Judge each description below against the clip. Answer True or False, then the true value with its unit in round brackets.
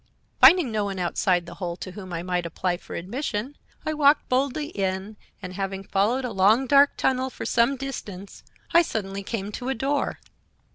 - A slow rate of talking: False (185 wpm)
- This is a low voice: False (210 Hz)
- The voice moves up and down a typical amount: False (6.0 semitones)